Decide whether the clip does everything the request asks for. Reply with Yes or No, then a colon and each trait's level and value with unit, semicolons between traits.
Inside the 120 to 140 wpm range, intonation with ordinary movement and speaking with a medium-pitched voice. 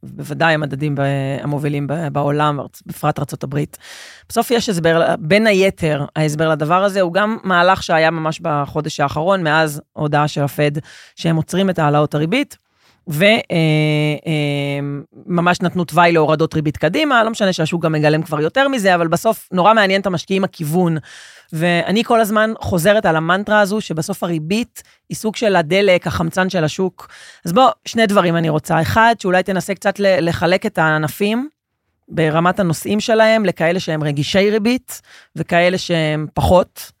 No: fast, 150 wpm; average, 4.3 semitones; medium, 170 Hz